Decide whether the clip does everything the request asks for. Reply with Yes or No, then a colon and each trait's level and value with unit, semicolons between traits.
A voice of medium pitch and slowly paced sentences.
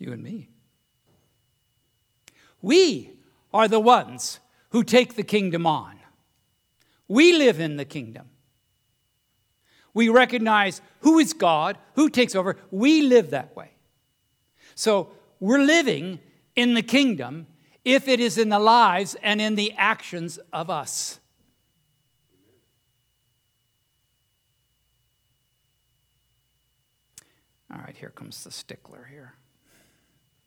Yes: medium, 165 Hz; slow, 105 wpm